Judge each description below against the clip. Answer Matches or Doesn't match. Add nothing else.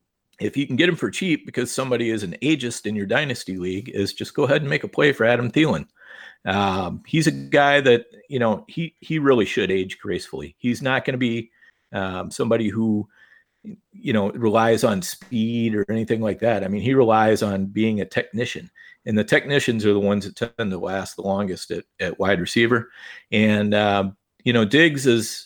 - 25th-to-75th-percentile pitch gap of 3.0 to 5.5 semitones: Matches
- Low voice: Matches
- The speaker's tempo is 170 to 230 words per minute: Matches